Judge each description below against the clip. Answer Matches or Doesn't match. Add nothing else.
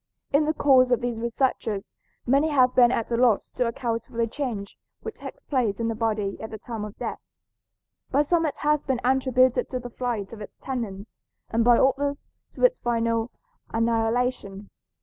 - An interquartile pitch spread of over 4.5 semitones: Doesn't match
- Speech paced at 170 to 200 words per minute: Matches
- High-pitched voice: Matches